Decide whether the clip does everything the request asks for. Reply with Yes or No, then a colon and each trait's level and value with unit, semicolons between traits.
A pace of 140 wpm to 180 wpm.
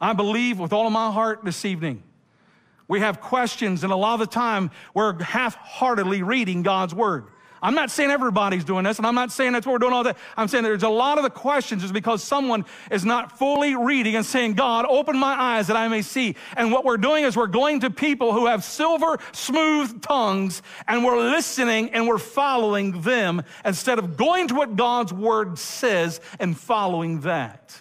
No: fast, 205 wpm